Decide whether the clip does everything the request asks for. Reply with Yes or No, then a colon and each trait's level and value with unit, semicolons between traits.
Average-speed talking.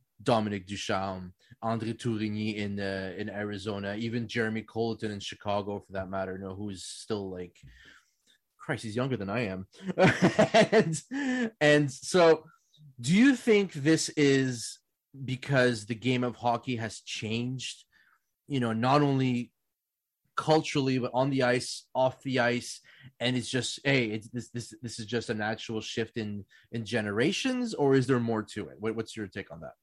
Yes: average, 165 wpm